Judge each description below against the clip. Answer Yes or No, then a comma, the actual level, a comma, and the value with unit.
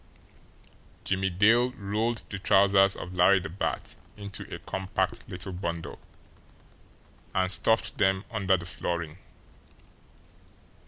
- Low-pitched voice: Yes, very low, 95 Hz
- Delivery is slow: Yes, slow, 110 wpm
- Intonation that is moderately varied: No, narrow, 1.8 semitones